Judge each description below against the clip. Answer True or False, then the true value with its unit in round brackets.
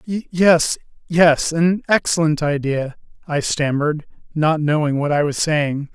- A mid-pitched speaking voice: True (155 Hz)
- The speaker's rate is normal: False (130 wpm)